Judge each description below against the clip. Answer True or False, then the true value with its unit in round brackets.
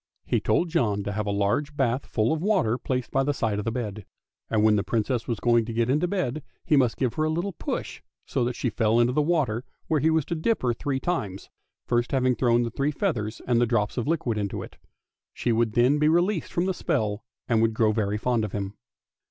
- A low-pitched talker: True (120 Hz)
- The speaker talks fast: True (240 wpm)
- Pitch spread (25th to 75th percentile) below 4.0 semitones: False (5.2 semitones)